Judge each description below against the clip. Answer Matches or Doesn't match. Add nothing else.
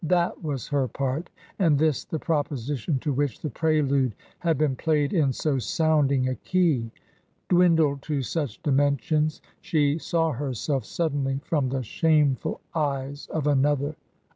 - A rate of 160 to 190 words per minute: Doesn't match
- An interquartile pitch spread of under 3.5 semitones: Matches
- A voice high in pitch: Doesn't match